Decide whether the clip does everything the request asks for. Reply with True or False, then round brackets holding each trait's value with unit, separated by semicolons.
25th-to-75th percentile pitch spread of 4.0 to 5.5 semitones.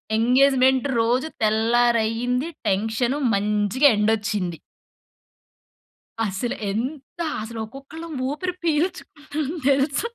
True (4.3 semitones)